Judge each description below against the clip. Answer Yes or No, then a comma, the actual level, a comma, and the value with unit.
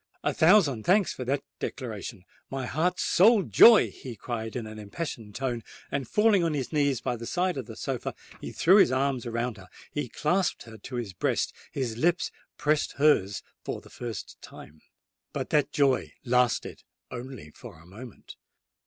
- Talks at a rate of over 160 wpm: Yes, average, 170 wpm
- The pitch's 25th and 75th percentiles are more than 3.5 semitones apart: Yes, average, 5.2 semitones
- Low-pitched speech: Yes, low, 130 Hz